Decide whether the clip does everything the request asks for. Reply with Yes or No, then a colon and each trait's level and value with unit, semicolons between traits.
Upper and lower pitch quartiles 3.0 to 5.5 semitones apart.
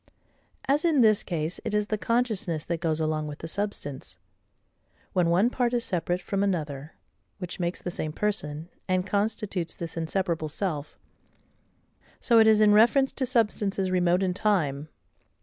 Yes: average, 4.7 semitones